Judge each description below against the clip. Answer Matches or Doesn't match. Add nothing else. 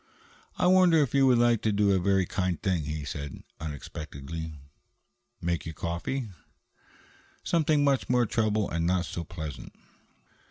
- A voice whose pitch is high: Doesn't match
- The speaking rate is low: Doesn't match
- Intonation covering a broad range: Matches